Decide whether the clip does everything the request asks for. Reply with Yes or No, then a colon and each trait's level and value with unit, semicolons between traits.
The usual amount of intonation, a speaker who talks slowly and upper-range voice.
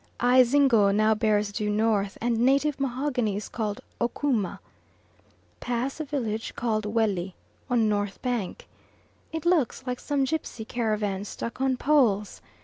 Yes: average, 3.9 semitones; slow, 130 wpm; high, 230 Hz